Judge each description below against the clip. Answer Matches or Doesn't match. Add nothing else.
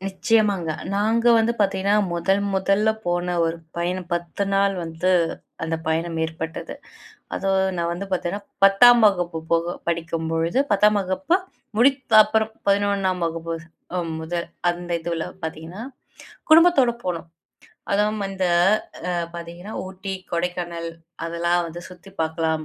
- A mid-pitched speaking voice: Matches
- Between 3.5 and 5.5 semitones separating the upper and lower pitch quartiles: Doesn't match